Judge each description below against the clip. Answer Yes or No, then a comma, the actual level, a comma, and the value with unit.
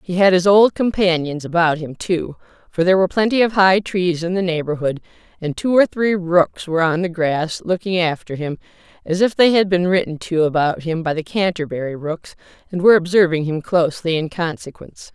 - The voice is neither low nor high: Yes, medium, 175 Hz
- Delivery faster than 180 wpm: Yes, average, 200 wpm